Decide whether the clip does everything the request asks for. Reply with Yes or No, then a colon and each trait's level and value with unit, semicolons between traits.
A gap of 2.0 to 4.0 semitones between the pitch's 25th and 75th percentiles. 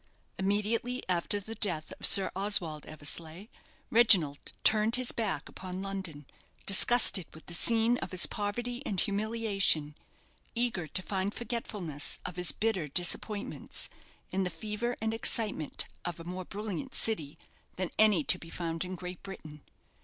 No: average, 4.5 semitones